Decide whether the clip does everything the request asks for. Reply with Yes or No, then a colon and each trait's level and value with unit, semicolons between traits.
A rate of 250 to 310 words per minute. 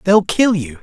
No: fast, 220 wpm